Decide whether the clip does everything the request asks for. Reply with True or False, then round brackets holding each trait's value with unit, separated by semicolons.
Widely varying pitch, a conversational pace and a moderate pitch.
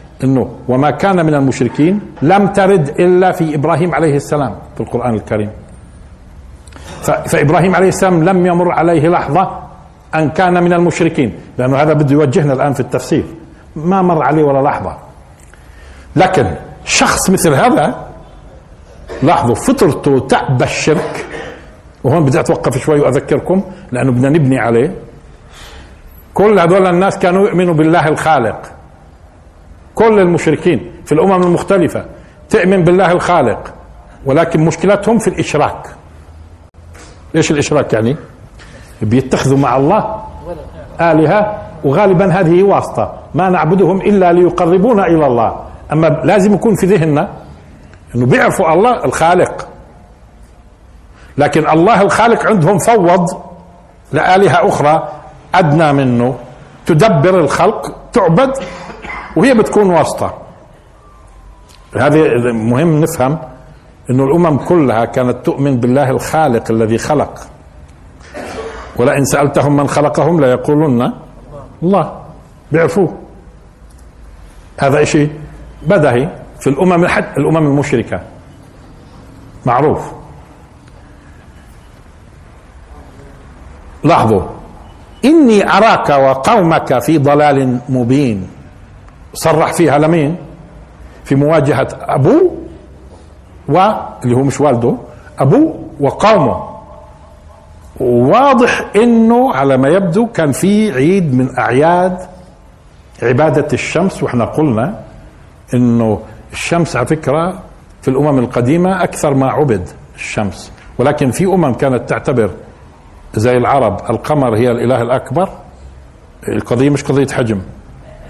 True (8.1 semitones; 100 wpm; 145 Hz)